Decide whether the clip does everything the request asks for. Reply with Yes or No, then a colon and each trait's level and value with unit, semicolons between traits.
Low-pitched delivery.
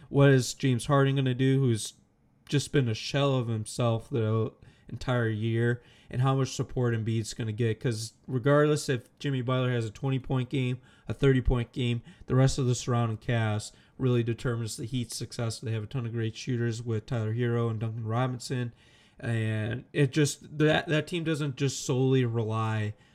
Yes: low, 125 Hz